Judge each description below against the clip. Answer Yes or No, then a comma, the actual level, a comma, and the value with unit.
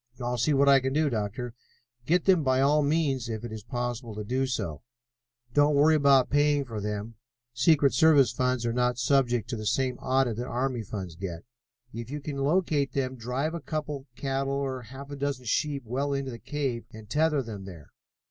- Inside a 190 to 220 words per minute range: Yes, fast, 205 wpm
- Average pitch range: Yes, average, 3.4 semitones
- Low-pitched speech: Yes, low, 130 Hz